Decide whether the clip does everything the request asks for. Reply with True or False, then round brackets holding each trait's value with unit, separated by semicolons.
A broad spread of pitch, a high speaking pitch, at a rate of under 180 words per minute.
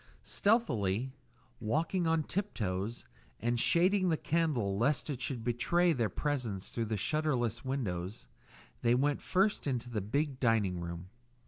False (6.5 semitones; 125 Hz; 140 wpm)